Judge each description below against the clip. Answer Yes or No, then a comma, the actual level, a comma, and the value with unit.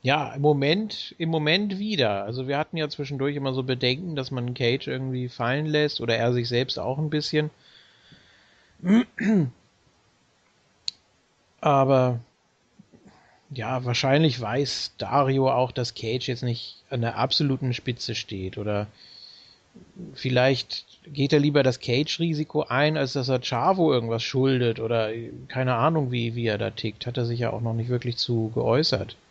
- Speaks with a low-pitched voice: Yes, low, 130 Hz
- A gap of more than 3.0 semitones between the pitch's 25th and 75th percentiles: Yes, average, 3.8 semitones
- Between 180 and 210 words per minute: No, average, 150 wpm